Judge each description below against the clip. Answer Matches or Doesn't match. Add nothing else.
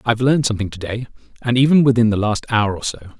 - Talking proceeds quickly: Matches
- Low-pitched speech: Matches